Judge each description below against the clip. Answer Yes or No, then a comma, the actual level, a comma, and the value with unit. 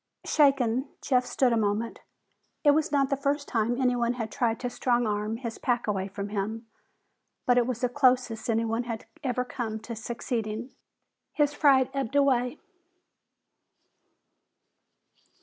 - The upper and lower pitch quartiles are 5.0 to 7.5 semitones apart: No, average, 2.9 semitones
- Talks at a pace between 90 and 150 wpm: Yes, average, 145 wpm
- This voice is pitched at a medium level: No, high, 245 Hz